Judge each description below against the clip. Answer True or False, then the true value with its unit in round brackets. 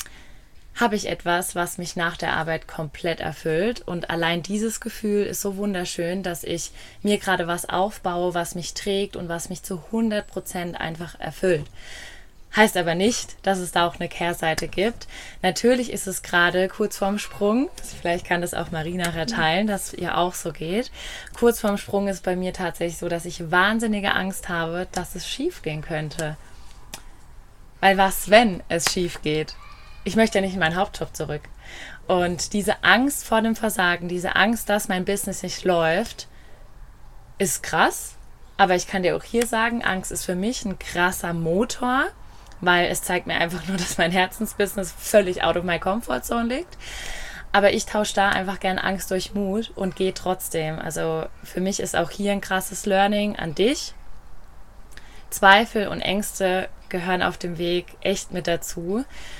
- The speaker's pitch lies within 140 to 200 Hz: True (185 Hz)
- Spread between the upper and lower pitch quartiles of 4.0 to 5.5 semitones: False (2.8 semitones)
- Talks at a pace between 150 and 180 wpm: True (175 wpm)